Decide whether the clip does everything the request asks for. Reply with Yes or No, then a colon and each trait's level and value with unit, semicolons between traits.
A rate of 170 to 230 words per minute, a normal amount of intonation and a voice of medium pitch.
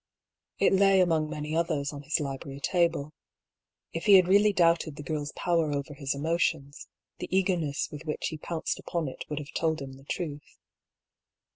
Yes: average, 175 wpm; average, 3.1 semitones; medium, 155 Hz